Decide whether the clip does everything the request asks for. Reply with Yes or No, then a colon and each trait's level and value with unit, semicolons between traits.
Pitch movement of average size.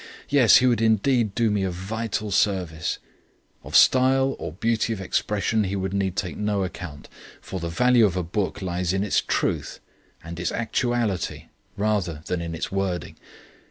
Yes: average, 3.8 semitones